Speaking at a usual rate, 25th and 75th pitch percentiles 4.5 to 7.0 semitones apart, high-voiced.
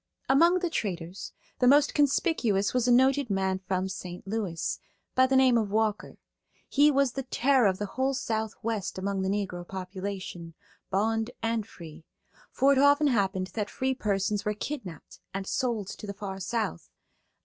Yes: average, 165 wpm; average, 5.3 semitones; high, 215 Hz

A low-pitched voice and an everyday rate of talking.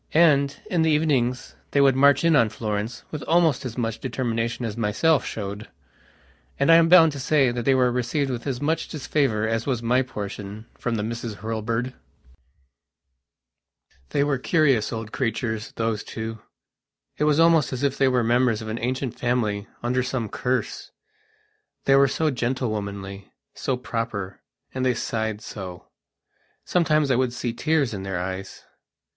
Yes: low, 125 Hz; average, 165 wpm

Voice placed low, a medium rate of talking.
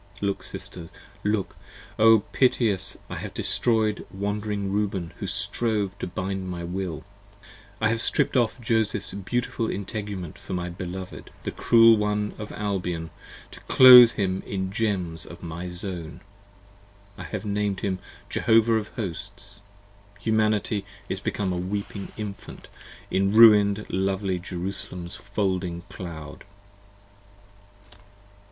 No: low, 100 Hz; slow, 125 wpm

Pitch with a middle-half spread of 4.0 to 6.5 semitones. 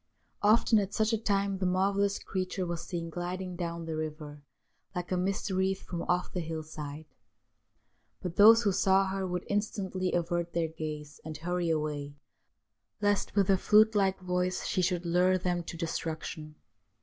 No: average, 2.7 semitones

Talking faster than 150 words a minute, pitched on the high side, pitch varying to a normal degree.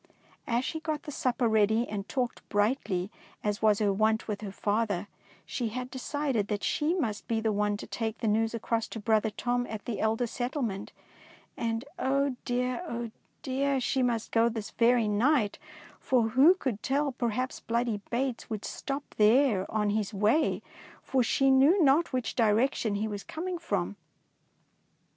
Yes: average, 180 wpm; high, 230 Hz; average, 3.6 semitones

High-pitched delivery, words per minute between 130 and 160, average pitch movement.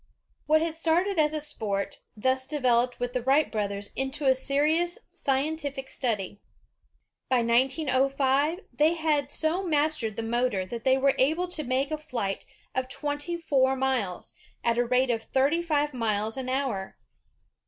Yes: very high, 265 Hz; average, 155 wpm; average, 3.9 semitones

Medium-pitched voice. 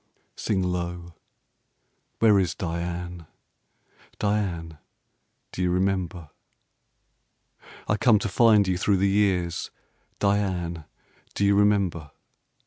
No: very low, 90 Hz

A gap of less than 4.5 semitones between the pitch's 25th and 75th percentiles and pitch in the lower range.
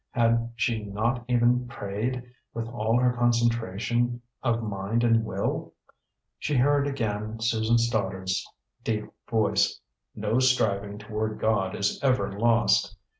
Yes: narrow, 2.4 semitones; low, 115 Hz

